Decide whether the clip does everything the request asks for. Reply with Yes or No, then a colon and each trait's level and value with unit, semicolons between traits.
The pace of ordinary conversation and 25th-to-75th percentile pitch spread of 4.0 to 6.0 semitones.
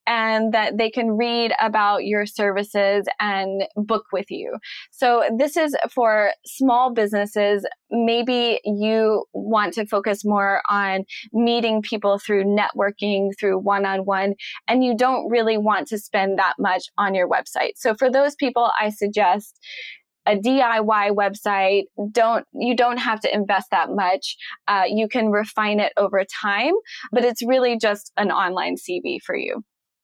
No: average, 150 wpm; average, 2.7 semitones